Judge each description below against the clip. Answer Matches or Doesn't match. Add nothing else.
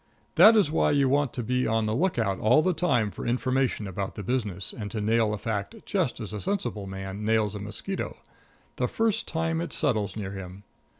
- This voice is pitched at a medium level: Doesn't match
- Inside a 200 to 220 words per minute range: Matches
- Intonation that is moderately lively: Doesn't match